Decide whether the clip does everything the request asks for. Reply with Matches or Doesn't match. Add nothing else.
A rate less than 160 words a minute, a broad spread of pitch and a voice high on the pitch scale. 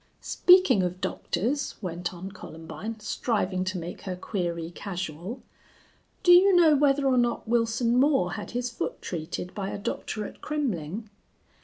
Matches